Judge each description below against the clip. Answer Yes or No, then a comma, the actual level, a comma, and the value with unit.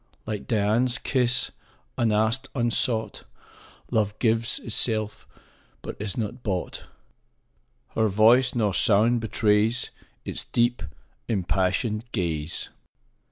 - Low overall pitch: Yes, low, 110 Hz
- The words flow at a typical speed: No, slow, 100 wpm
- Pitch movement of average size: No, narrow, 2.3 semitones